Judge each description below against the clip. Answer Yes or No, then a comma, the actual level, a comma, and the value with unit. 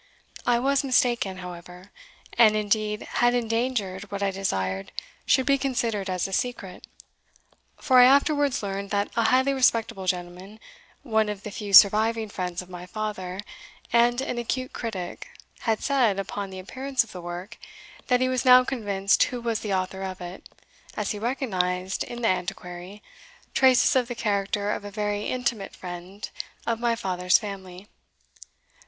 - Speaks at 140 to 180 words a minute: Yes, average, 160 wpm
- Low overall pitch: No, high, 210 Hz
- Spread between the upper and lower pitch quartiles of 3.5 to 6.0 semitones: Yes, average, 4.3 semitones